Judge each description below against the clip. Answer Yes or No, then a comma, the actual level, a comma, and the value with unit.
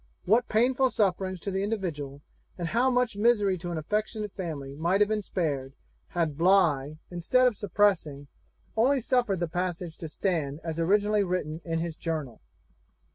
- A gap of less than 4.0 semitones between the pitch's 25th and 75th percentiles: No, average, 4.6 semitones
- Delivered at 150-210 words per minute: Yes, average, 160 wpm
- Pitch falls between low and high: Yes, medium, 180 Hz